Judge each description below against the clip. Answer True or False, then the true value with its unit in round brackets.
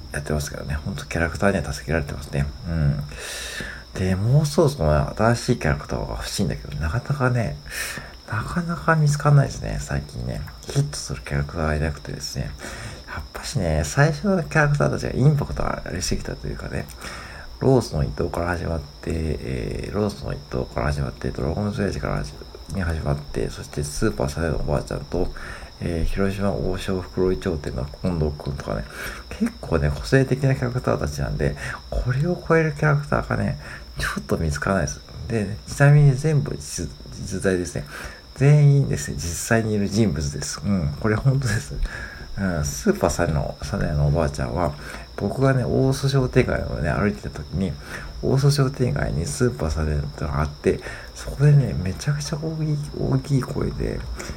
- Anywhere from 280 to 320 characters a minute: False (380 characters per minute)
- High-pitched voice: False (85 Hz)